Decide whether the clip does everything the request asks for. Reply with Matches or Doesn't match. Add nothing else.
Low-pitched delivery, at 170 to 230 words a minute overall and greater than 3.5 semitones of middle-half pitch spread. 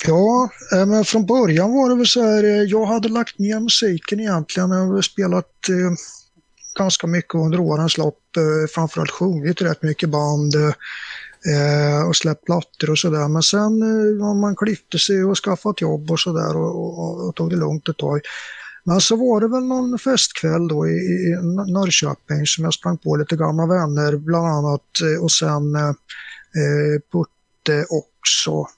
Doesn't match